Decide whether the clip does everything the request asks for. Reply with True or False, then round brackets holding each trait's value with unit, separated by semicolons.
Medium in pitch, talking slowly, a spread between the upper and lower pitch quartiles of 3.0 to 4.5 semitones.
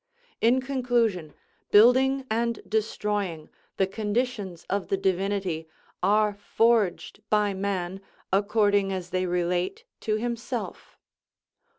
False (205 Hz; 100 wpm; 3.4 semitones)